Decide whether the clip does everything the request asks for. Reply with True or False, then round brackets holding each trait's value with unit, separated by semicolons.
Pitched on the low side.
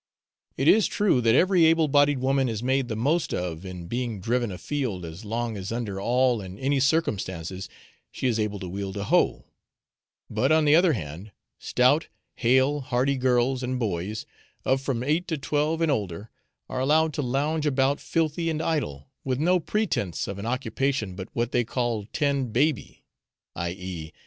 True (125 Hz)